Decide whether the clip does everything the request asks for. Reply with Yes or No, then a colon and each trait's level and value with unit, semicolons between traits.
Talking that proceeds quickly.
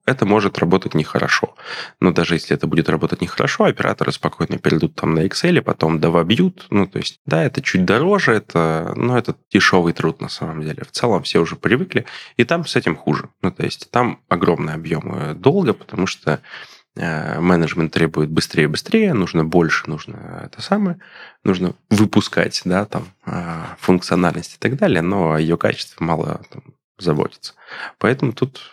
Yes: fast, 175 wpm